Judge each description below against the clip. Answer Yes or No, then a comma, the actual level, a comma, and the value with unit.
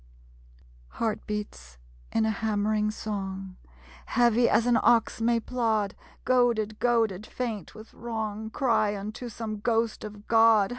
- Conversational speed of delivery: No, slow, 130 wpm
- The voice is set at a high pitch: Yes, high, 220 Hz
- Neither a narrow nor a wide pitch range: No, narrow, 1.8 semitones